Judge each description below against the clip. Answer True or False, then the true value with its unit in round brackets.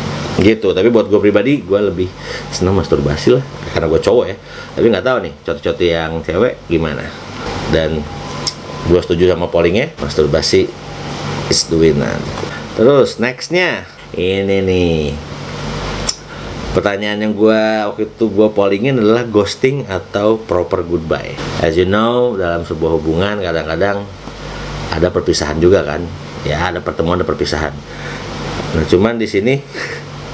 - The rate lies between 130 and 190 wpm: True (135 wpm)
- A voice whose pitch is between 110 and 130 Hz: False (95 Hz)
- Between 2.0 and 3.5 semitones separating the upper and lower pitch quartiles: False (4.9 semitones)